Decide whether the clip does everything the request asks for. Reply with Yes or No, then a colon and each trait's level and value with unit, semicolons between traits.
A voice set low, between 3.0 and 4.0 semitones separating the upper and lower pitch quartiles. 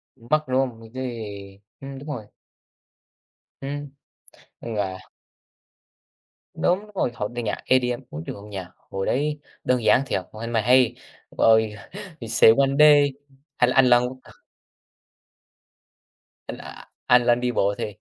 Yes: low, 120 Hz; average, 3.7 semitones